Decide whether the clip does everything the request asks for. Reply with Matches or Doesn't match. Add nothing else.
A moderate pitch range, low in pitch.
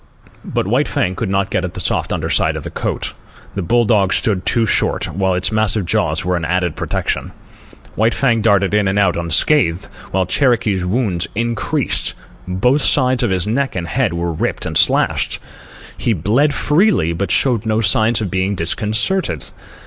Matches